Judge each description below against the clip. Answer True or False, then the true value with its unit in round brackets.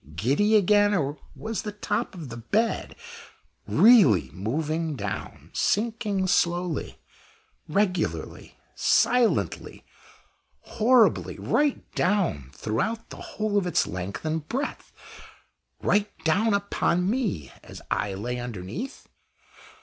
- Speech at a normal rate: False (105 wpm)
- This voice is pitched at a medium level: True (180 Hz)